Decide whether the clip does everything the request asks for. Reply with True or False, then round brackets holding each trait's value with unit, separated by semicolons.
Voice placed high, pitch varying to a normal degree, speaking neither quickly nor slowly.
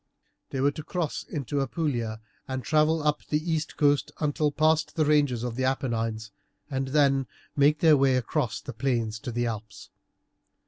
False (140 Hz; 3.9 semitones; 170 wpm)